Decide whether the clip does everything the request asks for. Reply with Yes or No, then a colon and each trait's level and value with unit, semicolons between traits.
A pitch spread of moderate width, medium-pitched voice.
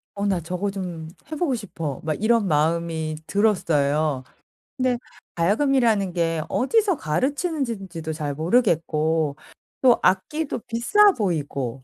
No: wide, 7.1 semitones; medium, 180 Hz